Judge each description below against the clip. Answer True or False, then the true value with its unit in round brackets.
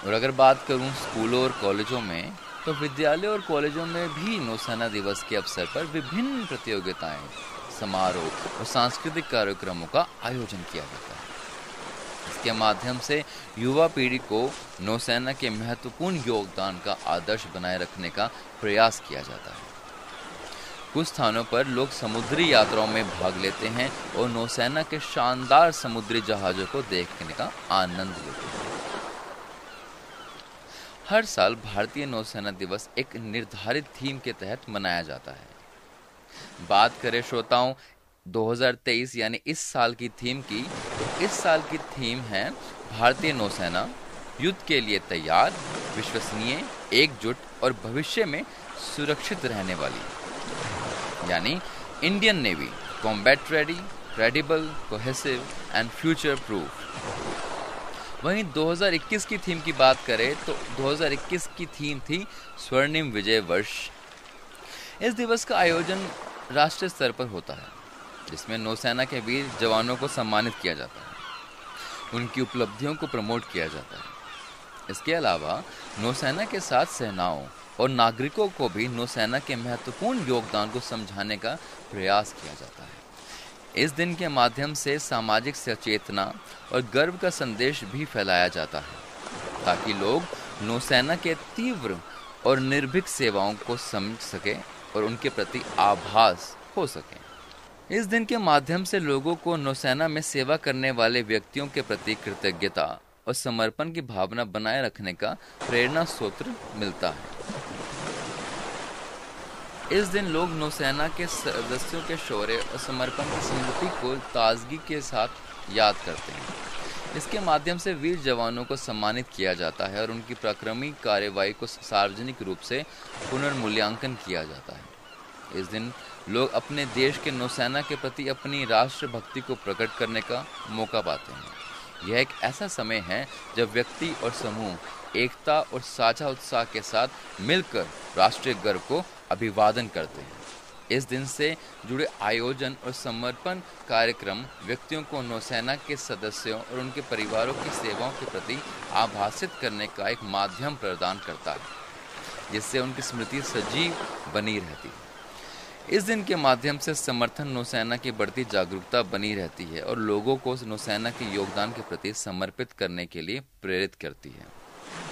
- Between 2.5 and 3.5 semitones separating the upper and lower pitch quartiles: False (5.1 semitones)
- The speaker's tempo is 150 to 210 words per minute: False (140 wpm)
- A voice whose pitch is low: True (125 Hz)